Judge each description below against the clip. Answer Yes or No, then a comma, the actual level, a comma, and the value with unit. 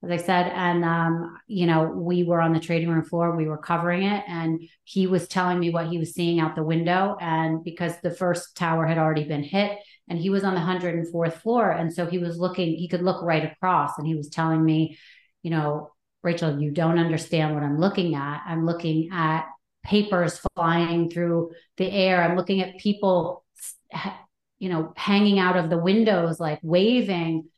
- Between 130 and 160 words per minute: No, average, 200 wpm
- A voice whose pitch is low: No, medium, 170 Hz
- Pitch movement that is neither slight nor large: No, narrow, 2.0 semitones